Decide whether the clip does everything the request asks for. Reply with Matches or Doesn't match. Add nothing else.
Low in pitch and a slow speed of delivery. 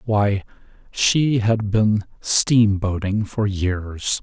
Matches